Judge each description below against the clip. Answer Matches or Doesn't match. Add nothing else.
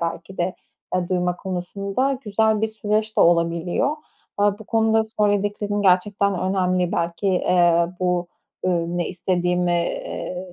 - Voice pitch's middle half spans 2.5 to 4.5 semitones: Matches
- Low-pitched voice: Doesn't match